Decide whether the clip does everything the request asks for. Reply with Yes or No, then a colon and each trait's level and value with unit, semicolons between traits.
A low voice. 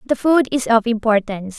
No: high, 230 Hz